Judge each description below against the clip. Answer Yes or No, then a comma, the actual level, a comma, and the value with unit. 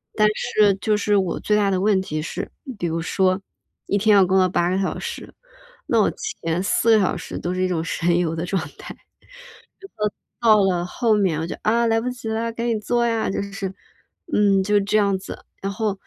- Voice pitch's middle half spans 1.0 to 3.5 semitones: Yes, average, 2.8 semitones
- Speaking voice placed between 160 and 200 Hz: Yes, high, 195 Hz